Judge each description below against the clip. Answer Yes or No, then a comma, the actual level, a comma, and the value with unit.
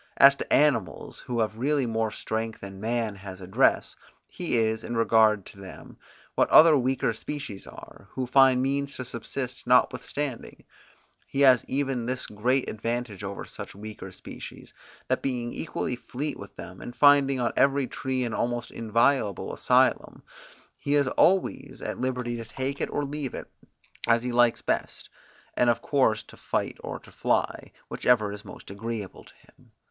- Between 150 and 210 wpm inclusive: Yes, average, 165 wpm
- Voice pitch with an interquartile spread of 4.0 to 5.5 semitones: No, average, 3.4 semitones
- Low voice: Yes, low, 120 Hz